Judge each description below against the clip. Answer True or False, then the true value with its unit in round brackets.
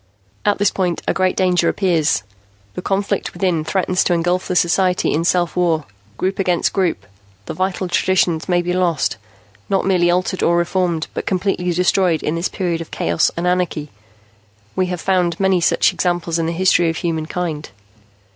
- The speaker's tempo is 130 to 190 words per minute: True (175 wpm)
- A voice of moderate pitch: True (180 Hz)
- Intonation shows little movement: True (1.8 semitones)